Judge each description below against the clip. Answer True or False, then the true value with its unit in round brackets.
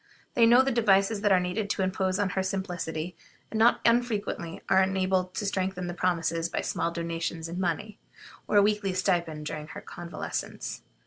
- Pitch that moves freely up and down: False (3.0 semitones)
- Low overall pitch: False (185 Hz)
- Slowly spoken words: False (180 wpm)